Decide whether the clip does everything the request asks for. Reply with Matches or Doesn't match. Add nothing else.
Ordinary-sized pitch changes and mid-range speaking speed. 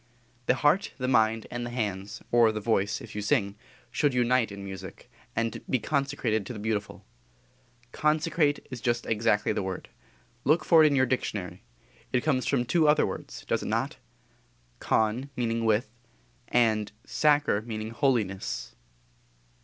Matches